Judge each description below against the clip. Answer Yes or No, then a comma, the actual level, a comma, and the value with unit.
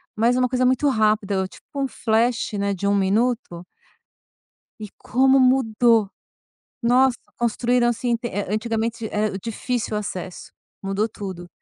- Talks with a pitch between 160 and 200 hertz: No, high, 225 Hz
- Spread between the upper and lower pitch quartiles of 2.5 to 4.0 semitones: Yes, average, 3.3 semitones